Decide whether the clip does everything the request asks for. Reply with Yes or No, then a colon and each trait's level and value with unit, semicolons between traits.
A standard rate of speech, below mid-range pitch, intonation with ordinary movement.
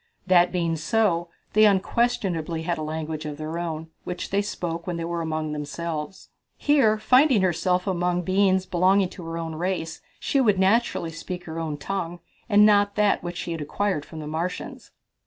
No: average, 180 wpm; medium, 175 Hz; average, 3.4 semitones